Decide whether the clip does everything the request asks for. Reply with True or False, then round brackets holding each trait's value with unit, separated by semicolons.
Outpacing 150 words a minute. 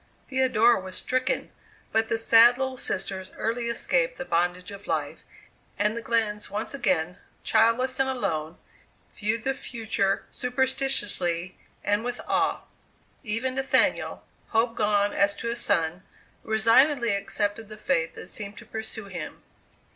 False (140 wpm)